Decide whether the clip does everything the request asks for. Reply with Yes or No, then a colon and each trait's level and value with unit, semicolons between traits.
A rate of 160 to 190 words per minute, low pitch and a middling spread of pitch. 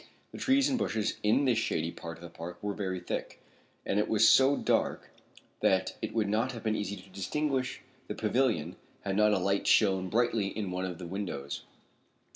No: average, 200 wpm; low, 105 Hz; average, 3.6 semitones